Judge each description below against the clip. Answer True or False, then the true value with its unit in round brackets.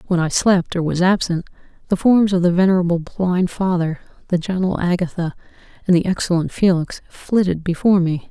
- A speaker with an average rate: True (165 wpm)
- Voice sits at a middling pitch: True (180 Hz)